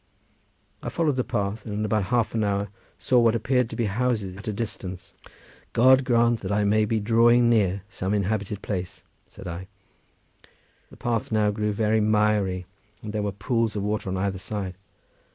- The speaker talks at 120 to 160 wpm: No, average, 185 wpm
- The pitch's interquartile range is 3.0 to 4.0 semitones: No, narrow, 2.5 semitones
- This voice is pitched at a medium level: No, low, 105 Hz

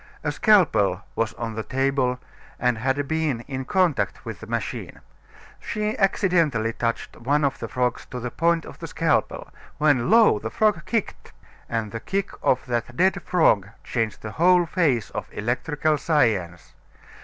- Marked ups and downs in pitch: Yes, wide, 6.5 semitones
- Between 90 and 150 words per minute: No, average, 160 wpm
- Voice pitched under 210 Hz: Yes, low, 135 Hz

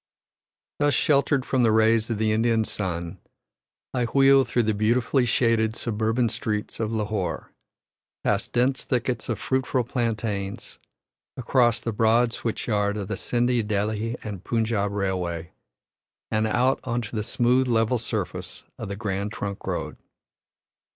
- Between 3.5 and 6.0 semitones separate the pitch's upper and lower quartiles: No, average, 2.7 semitones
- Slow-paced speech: No, average, 145 wpm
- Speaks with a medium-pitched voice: No, low, 110 Hz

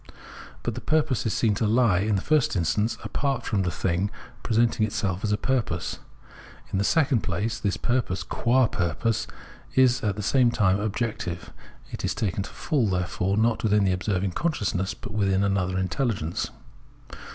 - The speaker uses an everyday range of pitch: Yes, average, 3.9 semitones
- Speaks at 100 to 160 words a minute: No, average, 170 wpm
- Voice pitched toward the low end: Yes, low, 105 Hz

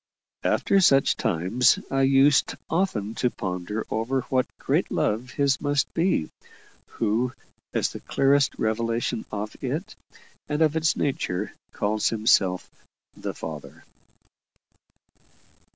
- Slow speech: Yes, slow, 115 wpm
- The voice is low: Yes, low, 120 Hz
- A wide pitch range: No, average, 4.6 semitones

